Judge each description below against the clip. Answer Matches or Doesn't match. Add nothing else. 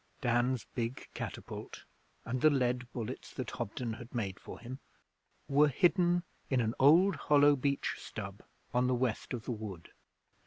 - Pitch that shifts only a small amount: Doesn't match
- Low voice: Matches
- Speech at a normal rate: Matches